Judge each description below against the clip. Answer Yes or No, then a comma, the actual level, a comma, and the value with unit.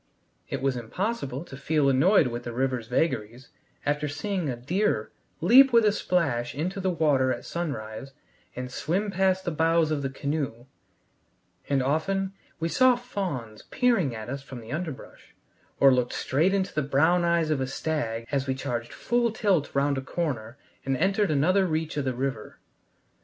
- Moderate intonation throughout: No, wide, 5.7 semitones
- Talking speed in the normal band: Yes, average, 175 wpm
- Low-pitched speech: No, medium, 145 Hz